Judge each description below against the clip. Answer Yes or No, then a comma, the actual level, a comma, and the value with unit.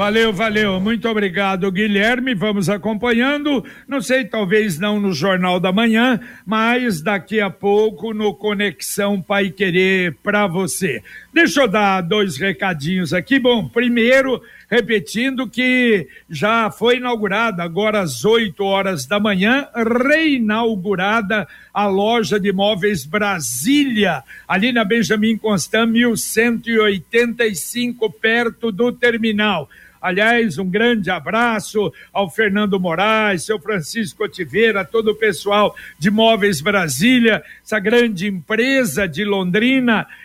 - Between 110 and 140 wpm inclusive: Yes, slow, 120 wpm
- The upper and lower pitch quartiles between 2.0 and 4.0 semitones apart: Yes, narrow, 2.6 semitones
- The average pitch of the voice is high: Yes, high, 215 Hz